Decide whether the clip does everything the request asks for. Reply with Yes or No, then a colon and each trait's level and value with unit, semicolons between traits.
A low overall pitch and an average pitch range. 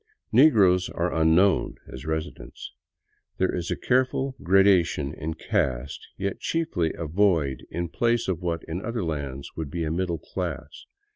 Yes: very low, 85 Hz; average, 3.8 semitones